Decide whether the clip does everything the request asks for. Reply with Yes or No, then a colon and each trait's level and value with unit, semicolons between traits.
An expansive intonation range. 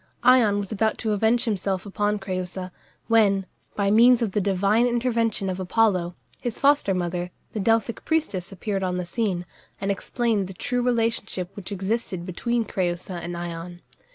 No: average, 3.7 semitones